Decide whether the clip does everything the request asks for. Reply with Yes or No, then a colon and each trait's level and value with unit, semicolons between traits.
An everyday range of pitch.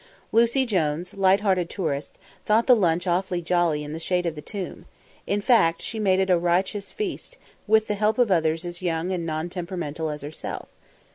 Yes: average, 3.7 semitones